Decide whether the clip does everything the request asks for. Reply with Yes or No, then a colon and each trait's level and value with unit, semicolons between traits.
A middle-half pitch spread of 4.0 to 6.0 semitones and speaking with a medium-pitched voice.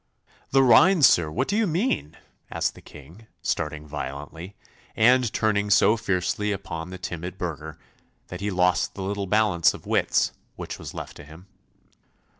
No: average, 5.1 semitones; very low, 95 Hz